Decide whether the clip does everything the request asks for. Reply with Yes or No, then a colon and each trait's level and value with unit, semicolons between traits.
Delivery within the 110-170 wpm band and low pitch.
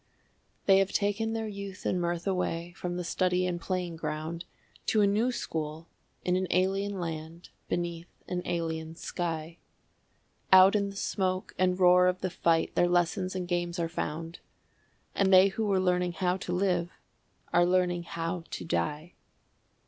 No: average, 165 wpm; medium, 180 Hz